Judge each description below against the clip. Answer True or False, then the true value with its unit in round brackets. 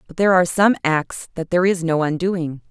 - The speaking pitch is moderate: True (170 Hz)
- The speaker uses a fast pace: True (220 wpm)